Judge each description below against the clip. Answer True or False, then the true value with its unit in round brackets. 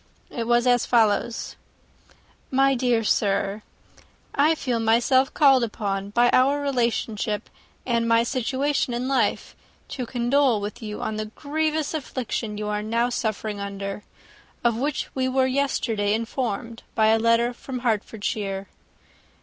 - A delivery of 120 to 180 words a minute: True (140 wpm)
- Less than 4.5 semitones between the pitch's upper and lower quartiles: True (3.3 semitones)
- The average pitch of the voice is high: True (235 Hz)